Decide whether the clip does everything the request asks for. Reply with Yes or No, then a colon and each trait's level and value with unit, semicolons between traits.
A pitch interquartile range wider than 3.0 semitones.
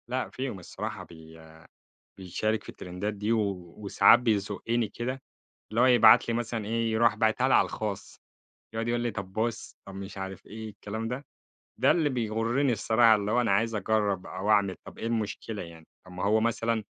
No: average, 2.7 semitones